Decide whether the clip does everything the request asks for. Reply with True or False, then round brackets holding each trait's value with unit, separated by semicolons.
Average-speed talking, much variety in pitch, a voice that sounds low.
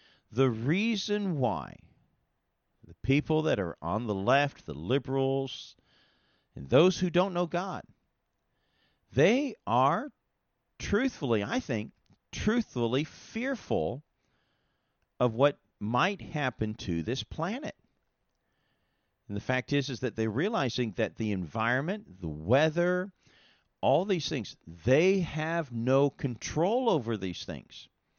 False (115 wpm; 7.3 semitones; 130 Hz)